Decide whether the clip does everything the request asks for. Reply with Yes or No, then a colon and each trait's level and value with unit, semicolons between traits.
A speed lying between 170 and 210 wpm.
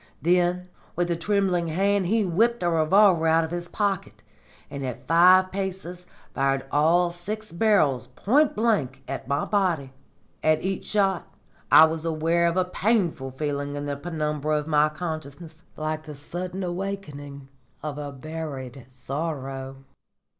No: average, 145 wpm